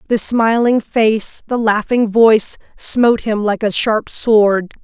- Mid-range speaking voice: No, high, 220 Hz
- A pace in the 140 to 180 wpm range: Yes, average, 150 wpm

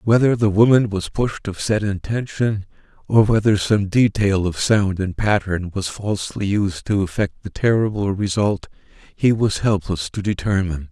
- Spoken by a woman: No, male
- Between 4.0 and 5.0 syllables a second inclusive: Yes, 4.6 syllables/s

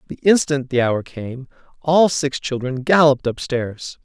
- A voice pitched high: No, low, 135 Hz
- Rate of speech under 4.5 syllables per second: Yes, 4.3 syllables/s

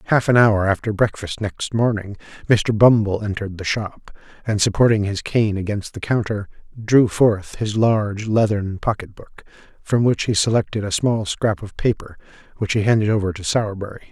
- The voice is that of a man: Yes, male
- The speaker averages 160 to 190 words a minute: Yes, average, 175 wpm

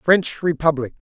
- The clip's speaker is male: Yes, male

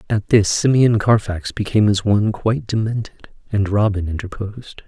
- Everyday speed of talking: Yes, average, 150 wpm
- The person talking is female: No, male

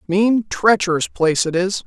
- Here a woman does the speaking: Yes, female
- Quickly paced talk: No, average, 160 wpm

